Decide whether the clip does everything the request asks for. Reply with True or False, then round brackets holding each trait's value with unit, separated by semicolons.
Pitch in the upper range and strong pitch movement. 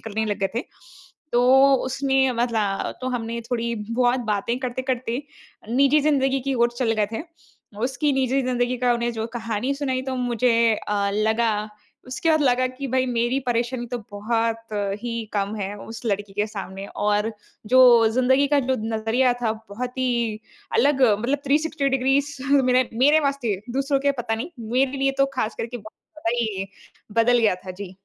False (245 Hz; 2.9 semitones)